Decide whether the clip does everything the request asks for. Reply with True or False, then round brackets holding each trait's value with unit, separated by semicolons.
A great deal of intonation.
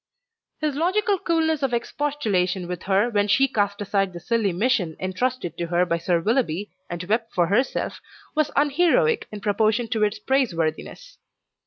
True (7.1 semitones)